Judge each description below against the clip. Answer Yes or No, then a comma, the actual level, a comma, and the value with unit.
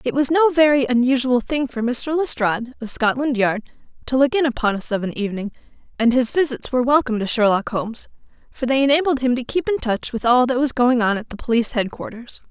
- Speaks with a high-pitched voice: Yes, very high, 250 Hz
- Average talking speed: No, fast, 220 wpm